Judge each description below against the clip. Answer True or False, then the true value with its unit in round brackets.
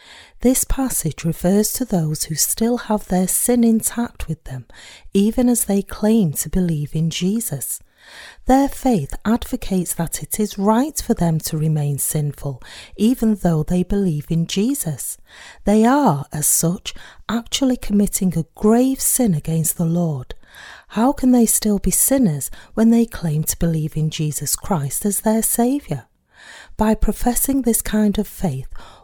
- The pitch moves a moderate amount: False (6.6 semitones)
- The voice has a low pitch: False (200 Hz)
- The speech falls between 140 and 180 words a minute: True (155 wpm)